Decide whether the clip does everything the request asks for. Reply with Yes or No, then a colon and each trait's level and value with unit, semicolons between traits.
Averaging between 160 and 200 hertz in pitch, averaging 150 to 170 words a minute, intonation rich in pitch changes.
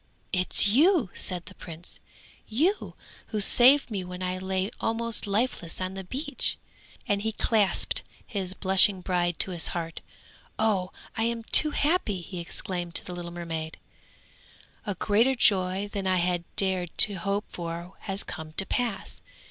No: high, 190 Hz; average, 160 wpm; average, 3.7 semitones